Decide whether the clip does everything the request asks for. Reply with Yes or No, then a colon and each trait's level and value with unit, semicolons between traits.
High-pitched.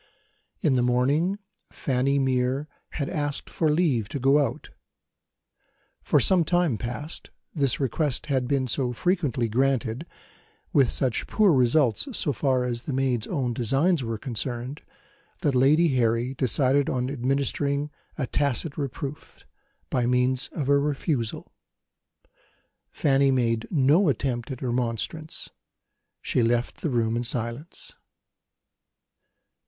No: low, 135 Hz